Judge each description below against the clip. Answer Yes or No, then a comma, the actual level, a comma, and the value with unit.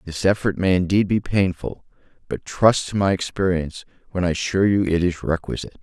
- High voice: No, very low, 90 Hz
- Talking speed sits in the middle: Yes, average, 185 wpm